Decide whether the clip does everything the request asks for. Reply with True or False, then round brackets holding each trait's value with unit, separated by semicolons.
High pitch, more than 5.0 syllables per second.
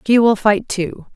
False (215 Hz; 4.2 syllables/s)